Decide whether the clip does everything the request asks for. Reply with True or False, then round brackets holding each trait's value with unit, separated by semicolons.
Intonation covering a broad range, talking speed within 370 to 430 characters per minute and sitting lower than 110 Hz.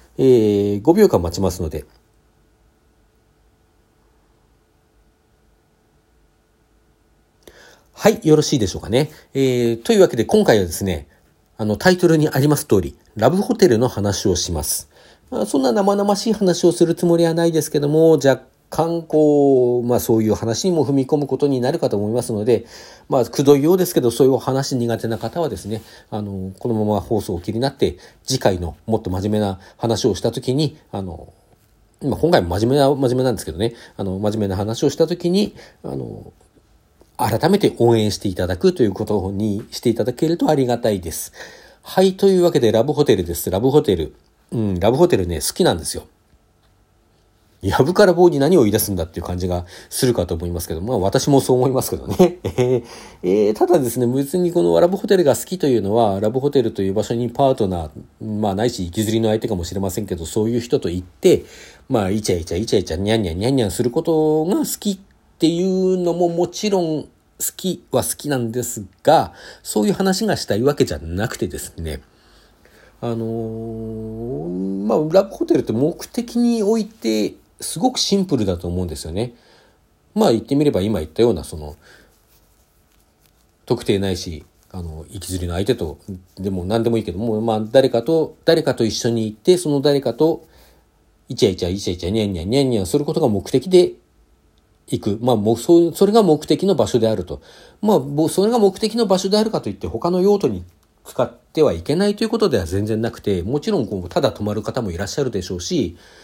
False (7.7 semitones; 375 characters per minute; 115 Hz)